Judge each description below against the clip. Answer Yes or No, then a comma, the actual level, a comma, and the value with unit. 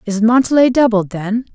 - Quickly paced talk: No, average, 155 wpm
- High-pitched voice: Yes, high, 225 Hz